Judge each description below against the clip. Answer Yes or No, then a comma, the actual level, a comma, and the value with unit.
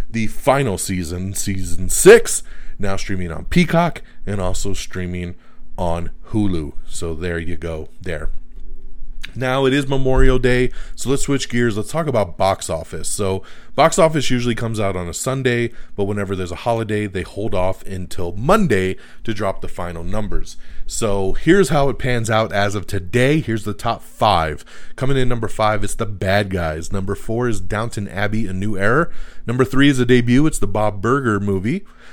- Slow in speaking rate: No, average, 180 wpm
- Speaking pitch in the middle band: No, low, 105 Hz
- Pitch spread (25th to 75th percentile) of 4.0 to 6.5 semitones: Yes, average, 4.8 semitones